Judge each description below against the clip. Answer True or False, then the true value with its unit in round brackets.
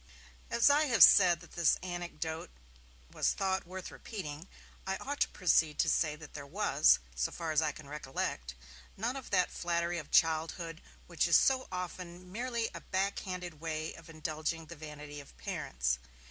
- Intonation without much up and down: False (3.4 semitones)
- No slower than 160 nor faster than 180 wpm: True (170 wpm)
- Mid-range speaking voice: True (170 Hz)